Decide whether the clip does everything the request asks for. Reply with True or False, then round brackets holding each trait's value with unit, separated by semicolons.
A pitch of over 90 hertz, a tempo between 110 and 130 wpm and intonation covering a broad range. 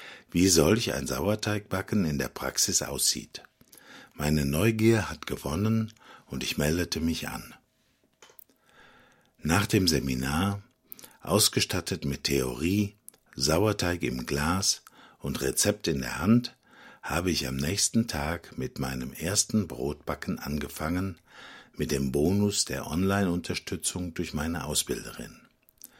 False (85 Hz; 115 wpm; 5.8 semitones)